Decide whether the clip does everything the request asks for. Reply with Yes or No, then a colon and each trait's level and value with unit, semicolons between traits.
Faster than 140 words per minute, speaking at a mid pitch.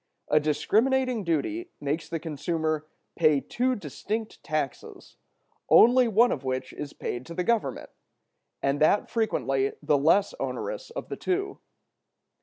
No: slow, 135 wpm; medium, 165 Hz